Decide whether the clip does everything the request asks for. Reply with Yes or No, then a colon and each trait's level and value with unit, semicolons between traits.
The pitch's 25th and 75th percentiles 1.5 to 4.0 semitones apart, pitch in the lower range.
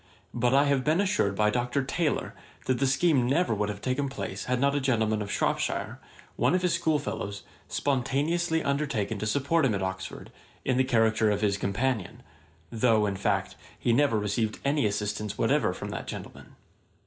No: average, 5.0 semitones; low, 125 Hz